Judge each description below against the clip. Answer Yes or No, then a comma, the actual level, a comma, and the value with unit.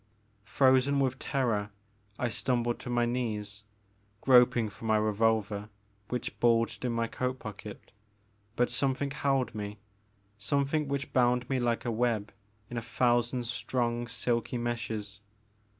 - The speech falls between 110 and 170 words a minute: Yes, slow, 135 wpm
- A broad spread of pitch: No, narrow, 2.6 semitones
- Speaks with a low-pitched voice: Yes, low, 120 Hz